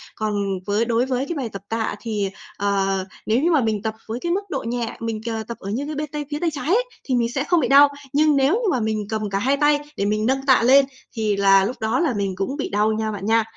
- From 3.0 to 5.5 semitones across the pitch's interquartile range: Yes, average, 4.8 semitones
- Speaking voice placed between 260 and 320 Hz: No, high, 230 Hz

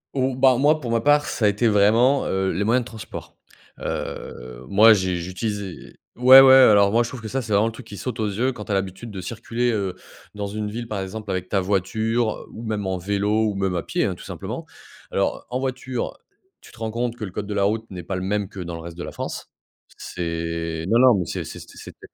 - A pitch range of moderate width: Yes, average, 3.7 semitones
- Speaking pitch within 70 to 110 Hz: Yes, low, 105 Hz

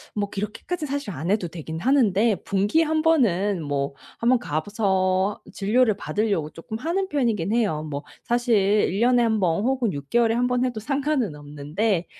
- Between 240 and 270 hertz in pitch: No, high, 210 Hz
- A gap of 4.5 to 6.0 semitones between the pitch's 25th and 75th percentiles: Yes, wide, 5.5 semitones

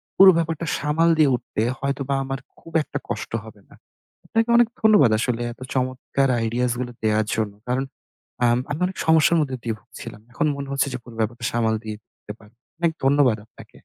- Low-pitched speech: Yes, low, 130 Hz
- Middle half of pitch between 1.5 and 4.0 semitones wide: No, average, 4.6 semitones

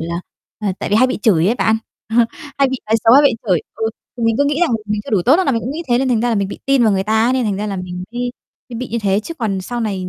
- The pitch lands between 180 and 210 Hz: No, high, 225 Hz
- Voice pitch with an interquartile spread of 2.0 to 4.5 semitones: Yes, average, 4.1 semitones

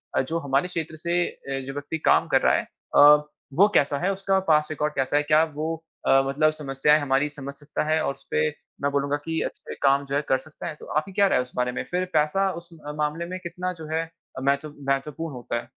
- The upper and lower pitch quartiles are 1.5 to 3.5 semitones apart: Yes, average, 3.0 semitones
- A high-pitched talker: No, medium, 150 Hz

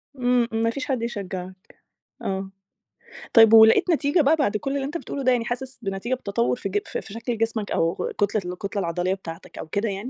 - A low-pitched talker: No, high, 225 Hz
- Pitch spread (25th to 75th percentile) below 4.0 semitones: No, average, 4.4 semitones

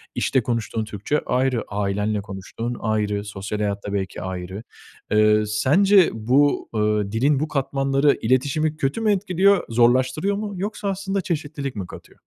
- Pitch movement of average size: No, wide, 6.4 semitones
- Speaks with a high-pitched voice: No, low, 125 Hz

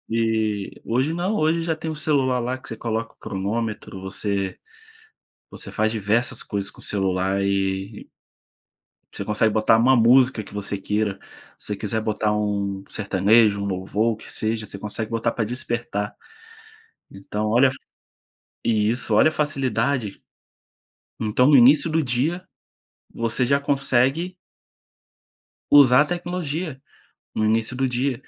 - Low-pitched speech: Yes, low, 115 Hz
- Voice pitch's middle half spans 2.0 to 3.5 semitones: No, average, 4.2 semitones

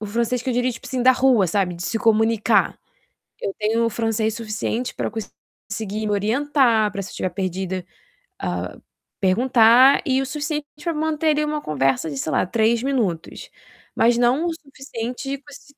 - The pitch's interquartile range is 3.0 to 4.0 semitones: No, average, 4.4 semitones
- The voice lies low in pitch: No, high, 230 Hz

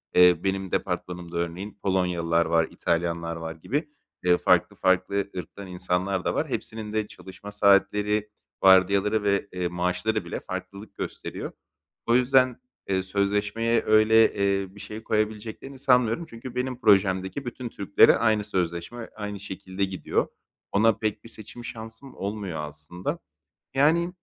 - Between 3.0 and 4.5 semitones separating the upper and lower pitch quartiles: Yes, average, 3.3 semitones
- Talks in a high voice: No, low, 100 Hz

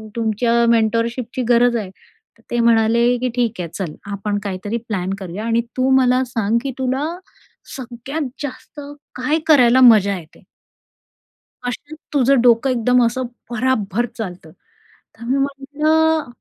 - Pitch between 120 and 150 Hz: No, high, 240 Hz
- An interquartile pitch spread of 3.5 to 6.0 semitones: No, average, 2.9 semitones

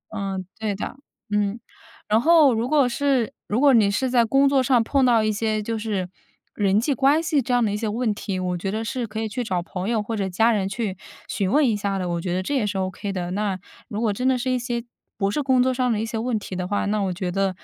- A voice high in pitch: Yes, high, 220 Hz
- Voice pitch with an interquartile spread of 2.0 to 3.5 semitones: No, average, 4.0 semitones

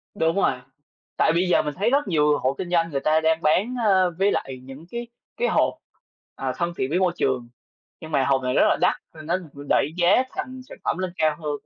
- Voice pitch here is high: No, medium, 165 Hz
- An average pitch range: Yes, average, 4.0 semitones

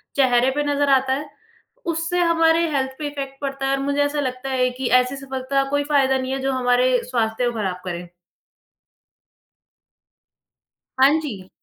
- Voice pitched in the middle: No, very high, 270 Hz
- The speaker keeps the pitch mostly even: Yes, narrow, 2.1 semitones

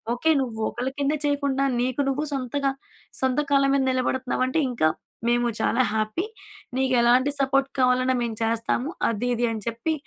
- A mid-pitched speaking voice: No, very high, 255 Hz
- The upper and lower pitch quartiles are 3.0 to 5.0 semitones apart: No, narrow, 2.4 semitones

